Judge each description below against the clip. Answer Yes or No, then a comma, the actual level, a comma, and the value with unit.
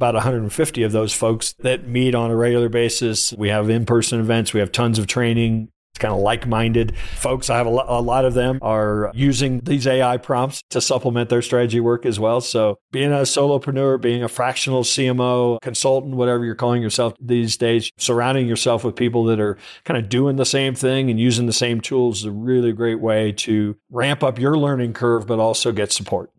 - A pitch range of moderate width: No, narrow, 2.2 semitones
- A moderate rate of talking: No, fast, 215 wpm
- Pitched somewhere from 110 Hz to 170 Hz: Yes, low, 120 Hz